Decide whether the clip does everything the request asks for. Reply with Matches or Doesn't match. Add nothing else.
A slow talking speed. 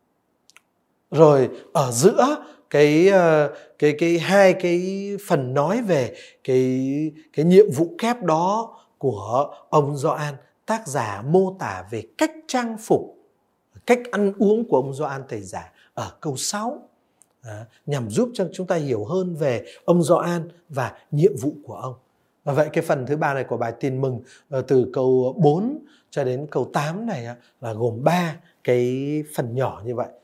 Matches